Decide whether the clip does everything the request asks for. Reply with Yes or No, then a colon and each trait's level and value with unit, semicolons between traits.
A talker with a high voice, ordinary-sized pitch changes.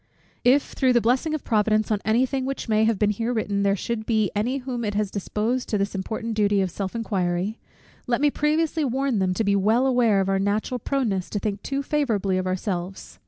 Yes: high, 220 Hz; average, 4.0 semitones